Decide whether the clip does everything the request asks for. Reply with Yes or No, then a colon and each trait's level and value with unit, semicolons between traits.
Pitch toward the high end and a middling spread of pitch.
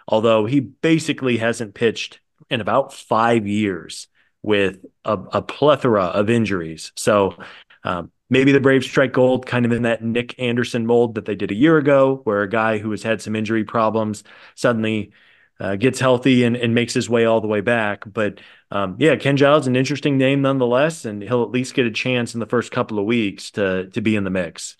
No: low, 115 Hz; average, 3.3 semitones